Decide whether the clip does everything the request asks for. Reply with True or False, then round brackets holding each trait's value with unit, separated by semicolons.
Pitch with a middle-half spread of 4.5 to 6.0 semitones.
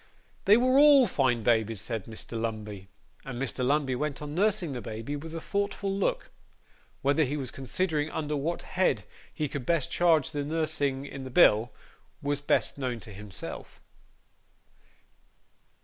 True (5.1 semitones)